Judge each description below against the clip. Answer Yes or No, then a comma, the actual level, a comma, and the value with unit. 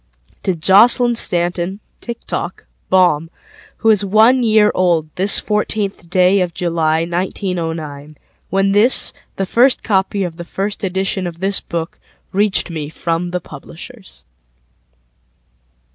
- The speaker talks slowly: Yes, slow, 115 wpm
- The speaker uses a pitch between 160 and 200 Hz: Yes, medium, 185 Hz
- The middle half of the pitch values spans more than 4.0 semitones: No, average, 3.3 semitones